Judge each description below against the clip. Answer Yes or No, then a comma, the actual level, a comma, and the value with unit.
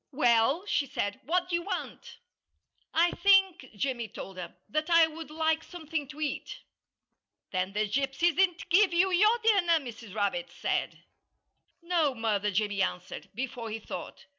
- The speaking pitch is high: Yes, very high, 295 Hz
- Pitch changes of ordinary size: No, wide, 7.5 semitones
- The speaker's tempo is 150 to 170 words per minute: Yes, average, 155 wpm